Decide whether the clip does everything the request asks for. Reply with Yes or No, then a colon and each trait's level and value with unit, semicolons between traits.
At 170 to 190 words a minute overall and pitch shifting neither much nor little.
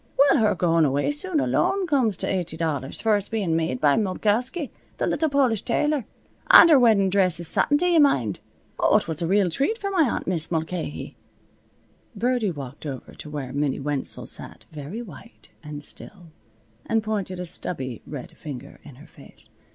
No: average, 185 wpm; wide, 8.2 semitones